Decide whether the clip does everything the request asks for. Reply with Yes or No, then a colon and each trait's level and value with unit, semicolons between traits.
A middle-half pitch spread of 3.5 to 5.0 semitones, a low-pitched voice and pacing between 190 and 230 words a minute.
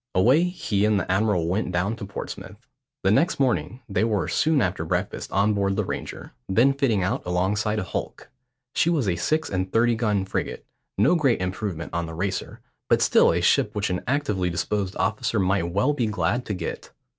Yes: average, 4.4 semitones; low, 105 Hz; average, 195 wpm